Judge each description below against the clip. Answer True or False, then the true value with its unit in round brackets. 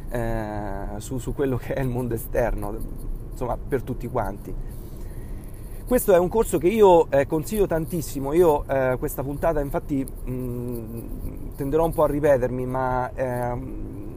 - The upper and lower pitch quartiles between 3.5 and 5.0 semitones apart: True (4.2 semitones)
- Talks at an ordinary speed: True (150 wpm)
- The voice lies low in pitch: True (125 Hz)